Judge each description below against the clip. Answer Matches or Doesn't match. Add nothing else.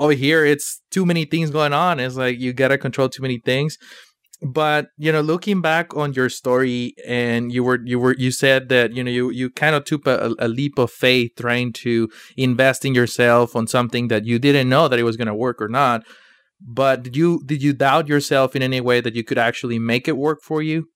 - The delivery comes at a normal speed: Doesn't match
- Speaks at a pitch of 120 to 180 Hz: Matches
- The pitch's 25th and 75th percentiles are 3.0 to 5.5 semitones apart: Matches